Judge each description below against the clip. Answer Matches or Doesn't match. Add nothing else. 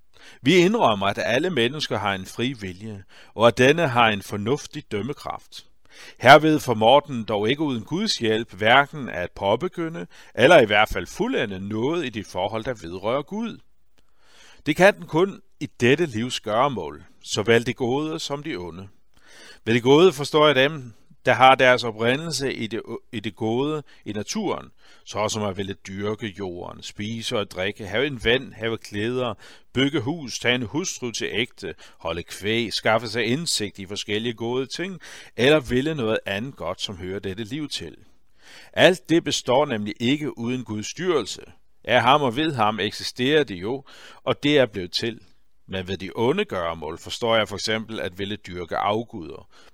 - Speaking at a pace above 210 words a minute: Doesn't match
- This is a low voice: Matches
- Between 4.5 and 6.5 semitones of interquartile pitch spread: Matches